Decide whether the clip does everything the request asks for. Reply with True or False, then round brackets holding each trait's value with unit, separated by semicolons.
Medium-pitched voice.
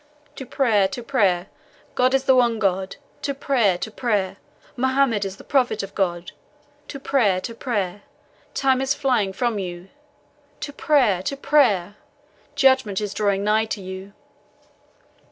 False (215 Hz)